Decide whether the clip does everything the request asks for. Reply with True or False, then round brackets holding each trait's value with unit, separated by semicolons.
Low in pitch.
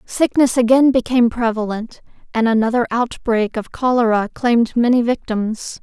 False (235 Hz)